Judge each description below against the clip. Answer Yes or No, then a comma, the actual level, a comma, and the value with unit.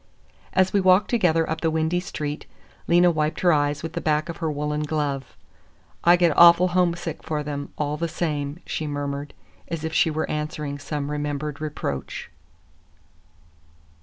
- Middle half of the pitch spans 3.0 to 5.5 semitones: No, narrow, 2.5 semitones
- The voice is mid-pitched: Yes, medium, 155 Hz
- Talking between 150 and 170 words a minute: Yes, average, 165 wpm